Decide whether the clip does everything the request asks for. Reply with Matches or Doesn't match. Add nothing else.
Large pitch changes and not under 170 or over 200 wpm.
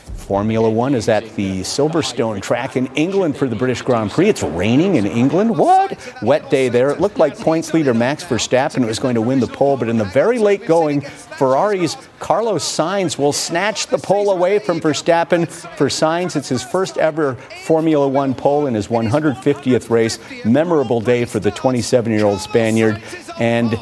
Matches